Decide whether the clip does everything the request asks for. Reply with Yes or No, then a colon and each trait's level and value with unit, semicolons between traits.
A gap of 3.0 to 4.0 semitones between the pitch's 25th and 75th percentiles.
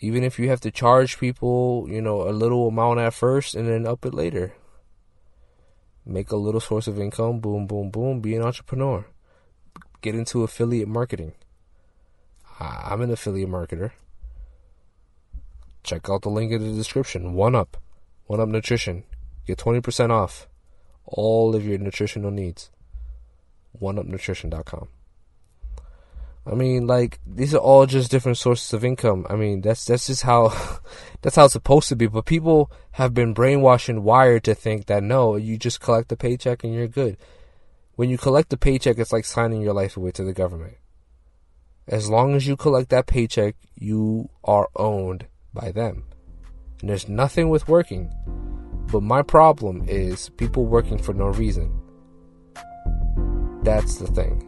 No: wide, 5.4 semitones